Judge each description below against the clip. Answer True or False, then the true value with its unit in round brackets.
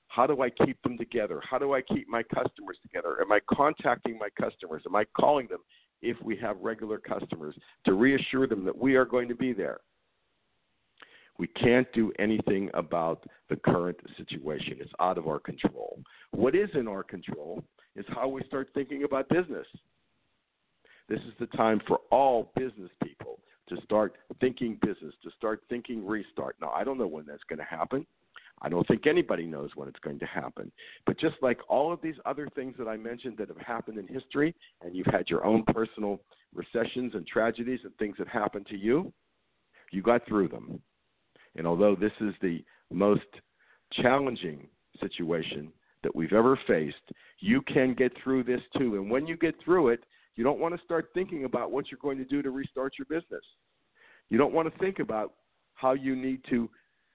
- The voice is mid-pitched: False (125 Hz)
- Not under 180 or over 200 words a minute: True (190 wpm)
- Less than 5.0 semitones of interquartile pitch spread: True (4.3 semitones)